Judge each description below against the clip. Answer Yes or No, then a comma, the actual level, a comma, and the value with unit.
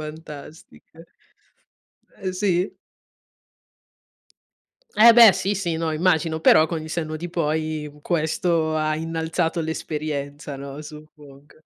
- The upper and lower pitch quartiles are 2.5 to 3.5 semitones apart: No, narrow, 2.0 semitones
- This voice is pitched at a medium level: Yes, medium, 160 Hz